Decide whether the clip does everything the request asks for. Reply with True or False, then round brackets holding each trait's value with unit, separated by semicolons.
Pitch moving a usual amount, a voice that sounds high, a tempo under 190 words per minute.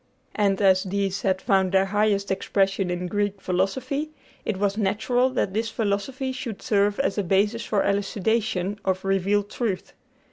False (1.9 semitones; 200 Hz; 165 wpm)